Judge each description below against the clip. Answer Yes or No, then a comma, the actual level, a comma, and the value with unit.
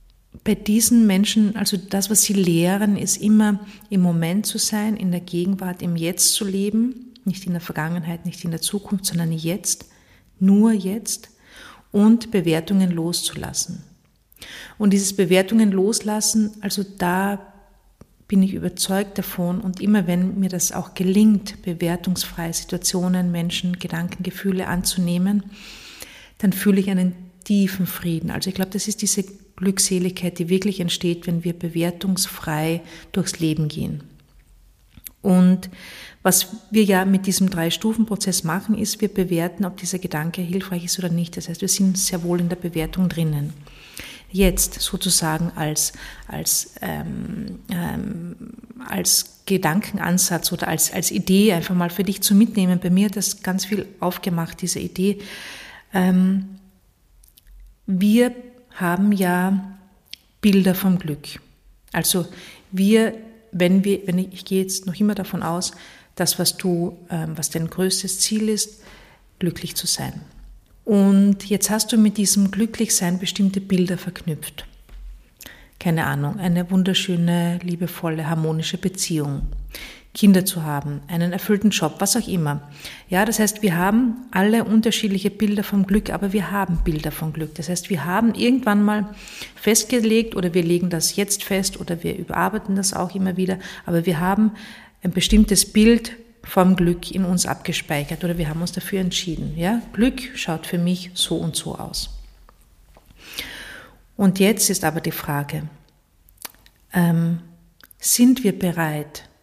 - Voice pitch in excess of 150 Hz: Yes, medium, 185 Hz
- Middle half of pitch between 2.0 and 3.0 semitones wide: Yes, average, 2.7 semitones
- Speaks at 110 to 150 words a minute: Yes, average, 145 wpm